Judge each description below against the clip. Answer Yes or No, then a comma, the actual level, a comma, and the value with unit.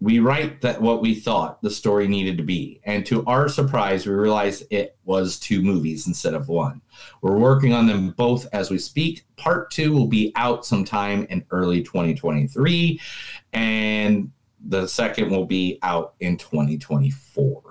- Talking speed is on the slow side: No, average, 180 wpm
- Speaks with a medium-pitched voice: No, low, 105 Hz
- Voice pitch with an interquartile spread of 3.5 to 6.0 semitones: Yes, average, 5.0 semitones